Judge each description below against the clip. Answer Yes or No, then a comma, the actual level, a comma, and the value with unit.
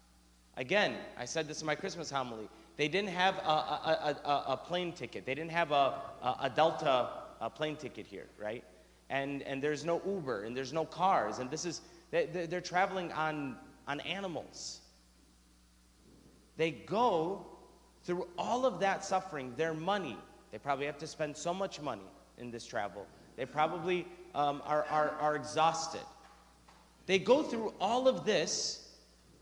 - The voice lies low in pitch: No, medium, 155 Hz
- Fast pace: No, average, 165 wpm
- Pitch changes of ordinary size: No, wide, 5.9 semitones